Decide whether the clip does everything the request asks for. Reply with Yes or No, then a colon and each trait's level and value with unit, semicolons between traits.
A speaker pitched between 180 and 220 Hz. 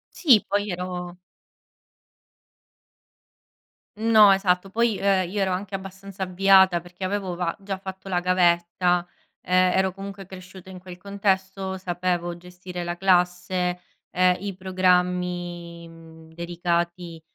Yes: medium, 185 Hz